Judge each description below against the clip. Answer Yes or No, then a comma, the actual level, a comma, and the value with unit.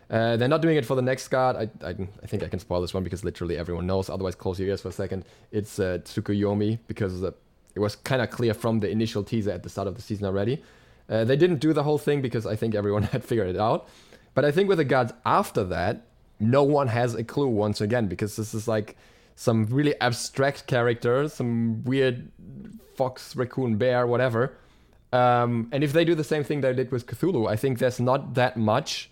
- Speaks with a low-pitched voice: Yes, low, 115 Hz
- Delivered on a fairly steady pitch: No, average, 3.8 semitones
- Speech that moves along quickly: Yes, fast, 230 wpm